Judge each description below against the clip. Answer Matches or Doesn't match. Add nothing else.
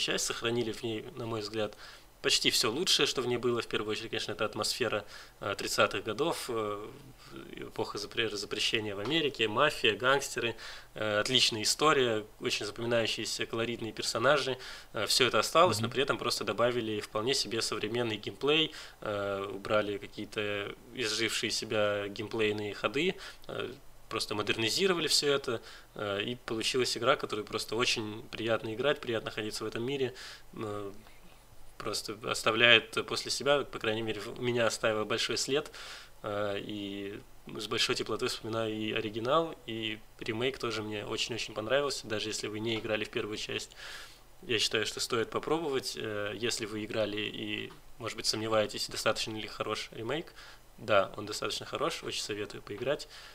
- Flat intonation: Matches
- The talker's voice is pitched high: Doesn't match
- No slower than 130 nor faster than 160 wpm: Matches